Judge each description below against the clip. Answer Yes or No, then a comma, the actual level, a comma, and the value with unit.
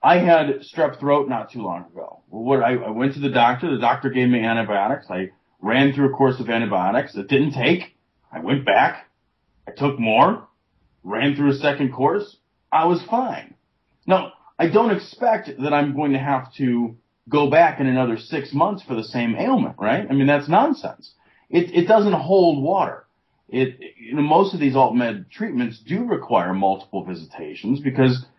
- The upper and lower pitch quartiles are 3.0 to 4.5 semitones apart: No, average, 5.1 semitones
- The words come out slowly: No, average, 180 wpm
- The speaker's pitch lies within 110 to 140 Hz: Yes, low, 135 Hz